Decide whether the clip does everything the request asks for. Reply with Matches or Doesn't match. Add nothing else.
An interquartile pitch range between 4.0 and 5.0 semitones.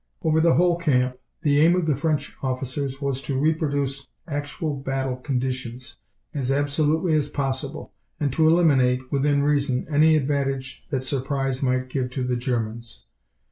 Doesn't match